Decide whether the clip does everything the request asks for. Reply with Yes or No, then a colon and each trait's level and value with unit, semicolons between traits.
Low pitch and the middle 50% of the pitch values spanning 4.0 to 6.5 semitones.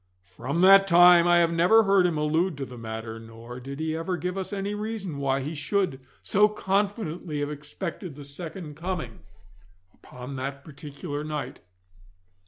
No: medium, 160 Hz; average, 5.1 semitones